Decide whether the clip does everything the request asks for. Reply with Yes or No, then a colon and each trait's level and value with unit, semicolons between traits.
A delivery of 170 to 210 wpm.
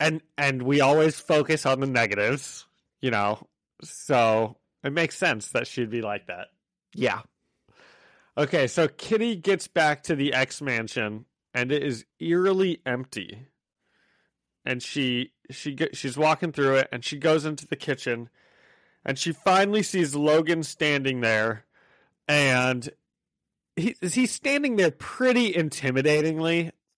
No: slow, 135 wpm